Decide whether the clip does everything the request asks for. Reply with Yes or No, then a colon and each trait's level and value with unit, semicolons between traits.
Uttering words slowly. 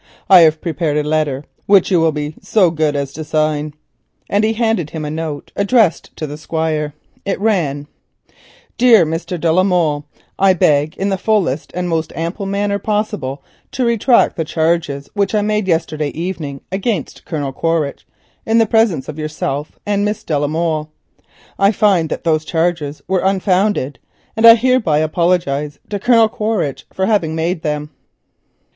No: average, 170 wpm